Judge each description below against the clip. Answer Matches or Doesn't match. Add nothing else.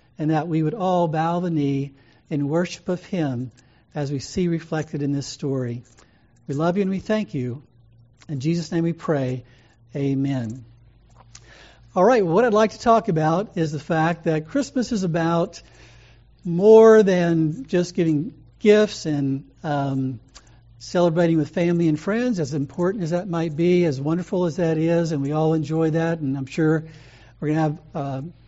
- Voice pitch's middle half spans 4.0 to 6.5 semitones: Matches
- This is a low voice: Doesn't match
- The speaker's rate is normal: Matches